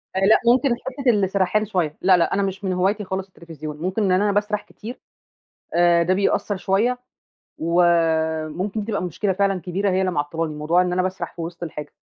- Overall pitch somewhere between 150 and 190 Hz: Yes, medium, 185 Hz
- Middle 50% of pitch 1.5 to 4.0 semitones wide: Yes, average, 3.0 semitones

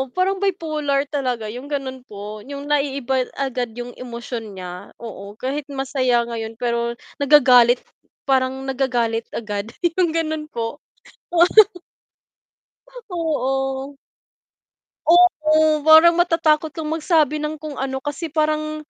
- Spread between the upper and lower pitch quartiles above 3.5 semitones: Yes, average, 4.1 semitones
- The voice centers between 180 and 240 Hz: No, very high, 275 Hz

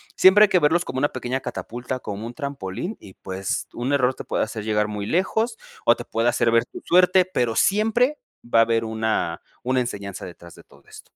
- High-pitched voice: No, low, 120 Hz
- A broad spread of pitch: Yes, wide, 8.1 semitones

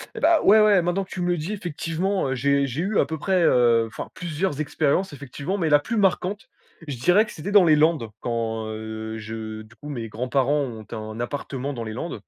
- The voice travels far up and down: Yes, wide, 7.4 semitones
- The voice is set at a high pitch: No, medium, 145 Hz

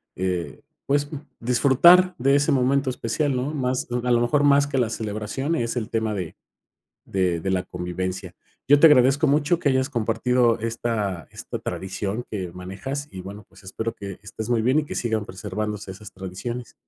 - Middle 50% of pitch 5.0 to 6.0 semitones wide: Yes, wide, 5.6 semitones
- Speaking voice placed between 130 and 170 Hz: No, low, 115 Hz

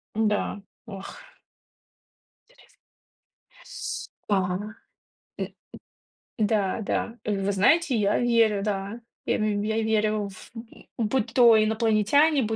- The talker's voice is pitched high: Yes, high, 215 Hz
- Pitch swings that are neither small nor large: No, narrow, 2.0 semitones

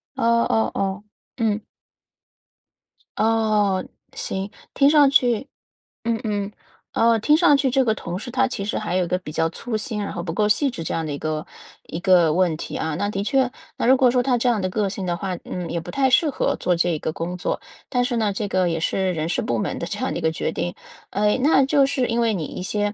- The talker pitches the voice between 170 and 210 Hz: Yes, high, 205 Hz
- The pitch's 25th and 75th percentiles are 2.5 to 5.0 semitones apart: No, wide, 5.6 semitones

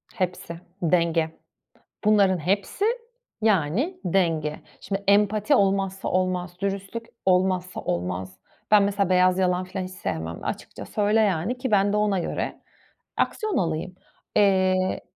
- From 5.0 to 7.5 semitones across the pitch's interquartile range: No, narrow, 2.4 semitones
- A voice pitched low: No, medium, 185 Hz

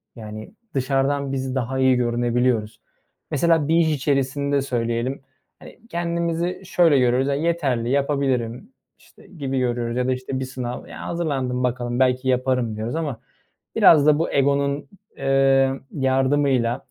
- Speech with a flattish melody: Yes, narrow, 2.3 semitones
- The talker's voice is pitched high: No, low, 135 Hz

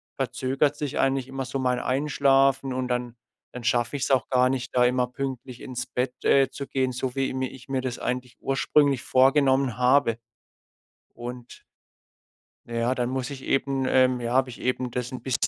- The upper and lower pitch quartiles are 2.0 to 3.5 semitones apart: No, narrow, 1.4 semitones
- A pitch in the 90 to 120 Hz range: No, low, 130 Hz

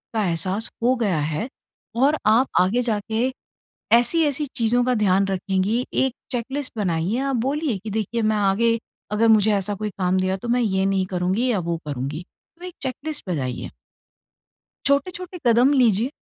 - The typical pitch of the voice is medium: No, high, 220 Hz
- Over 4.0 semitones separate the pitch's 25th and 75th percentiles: Yes, average, 4.9 semitones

